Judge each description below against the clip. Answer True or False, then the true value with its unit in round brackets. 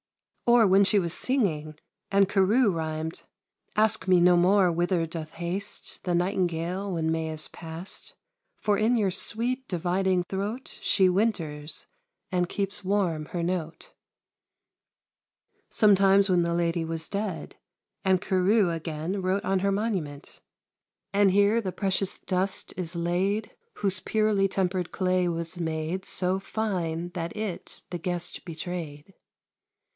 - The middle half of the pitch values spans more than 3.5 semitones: False (2.9 semitones)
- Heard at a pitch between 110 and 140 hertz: False (185 Hz)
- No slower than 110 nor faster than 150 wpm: True (135 wpm)